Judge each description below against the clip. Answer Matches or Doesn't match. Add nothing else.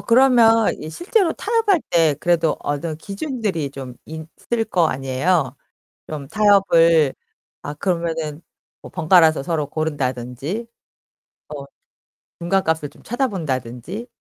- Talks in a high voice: Doesn't match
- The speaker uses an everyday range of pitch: Doesn't match